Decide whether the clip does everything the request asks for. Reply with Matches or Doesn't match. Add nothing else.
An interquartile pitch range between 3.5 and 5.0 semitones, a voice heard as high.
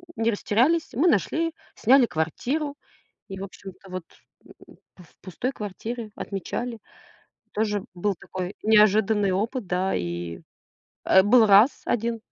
Matches